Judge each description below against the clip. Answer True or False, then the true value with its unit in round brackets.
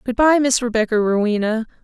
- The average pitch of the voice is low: False (235 Hz)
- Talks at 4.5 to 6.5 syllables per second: True (5.7 syllables/s)